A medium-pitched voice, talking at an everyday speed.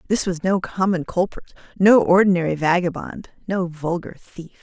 Yes: medium, 180 Hz; average, 145 wpm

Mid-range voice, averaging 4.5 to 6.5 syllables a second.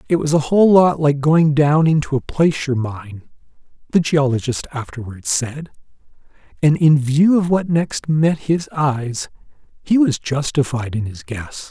No: medium, 145 Hz; 4.3 syllables/s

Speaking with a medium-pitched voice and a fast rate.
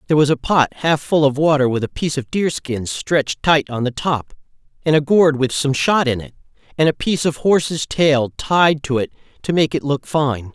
Yes: medium, 145 Hz; fast, 235 wpm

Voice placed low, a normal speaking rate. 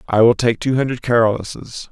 Yes: low, 115 Hz; average, 190 wpm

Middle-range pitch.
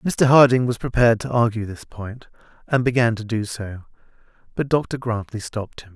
No: low, 115 Hz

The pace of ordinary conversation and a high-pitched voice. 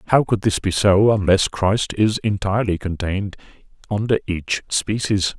No: average, 145 wpm; low, 100 Hz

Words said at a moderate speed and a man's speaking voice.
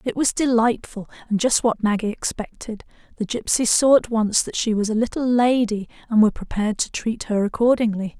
No: average, 190 wpm; female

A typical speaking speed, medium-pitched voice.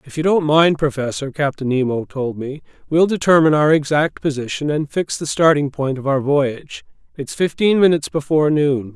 Yes: average, 180 wpm; medium, 150 Hz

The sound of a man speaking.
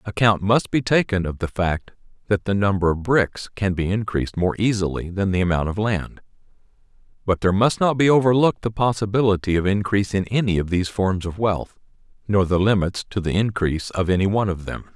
Yes: male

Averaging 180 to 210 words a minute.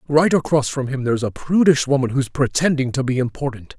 Yes: fast, 205 wpm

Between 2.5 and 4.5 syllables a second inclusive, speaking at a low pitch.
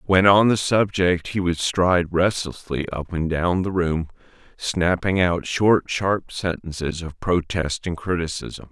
Yes: 4.0 syllables/s; very low, 90 Hz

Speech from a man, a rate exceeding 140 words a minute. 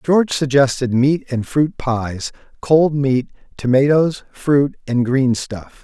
No: male; slow, 135 wpm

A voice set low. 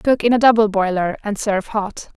No: high, 210 Hz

